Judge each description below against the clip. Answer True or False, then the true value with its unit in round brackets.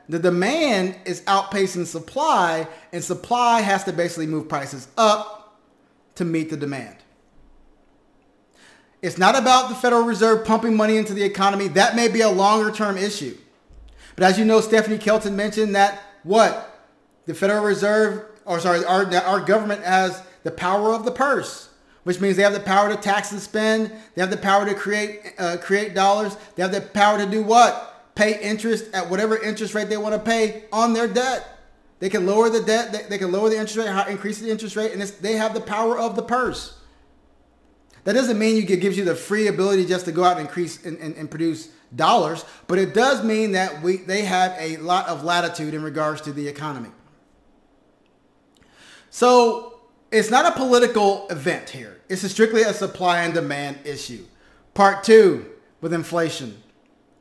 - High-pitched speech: True (200 Hz)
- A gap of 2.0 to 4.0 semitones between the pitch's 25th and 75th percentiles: True (3.5 semitones)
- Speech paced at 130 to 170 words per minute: False (185 wpm)